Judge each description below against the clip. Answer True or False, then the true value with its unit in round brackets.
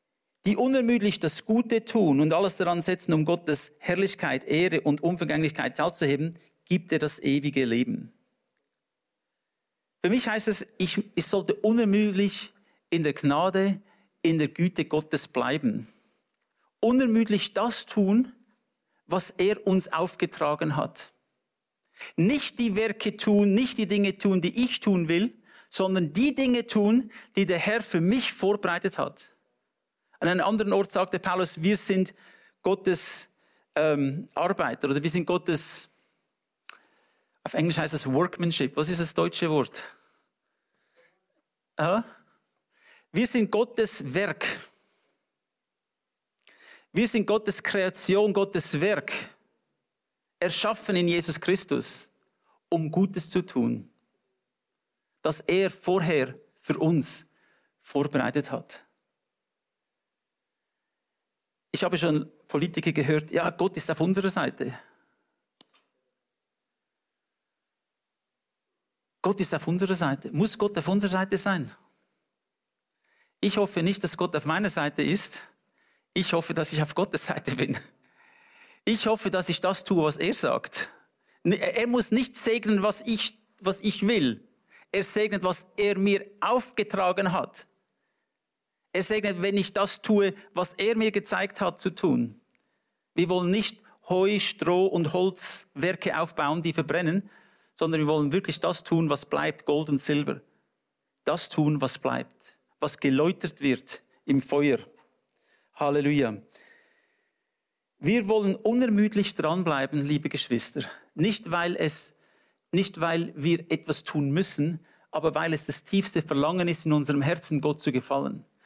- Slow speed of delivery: True (130 wpm)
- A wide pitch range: False (4.6 semitones)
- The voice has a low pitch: False (185 Hz)